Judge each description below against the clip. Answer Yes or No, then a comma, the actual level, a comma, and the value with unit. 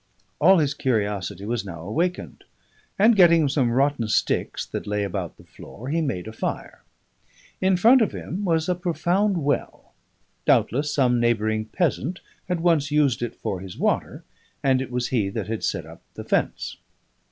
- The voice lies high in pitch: No, low, 135 Hz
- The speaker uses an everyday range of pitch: No, wide, 7.6 semitones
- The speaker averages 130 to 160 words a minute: No, average, 170 wpm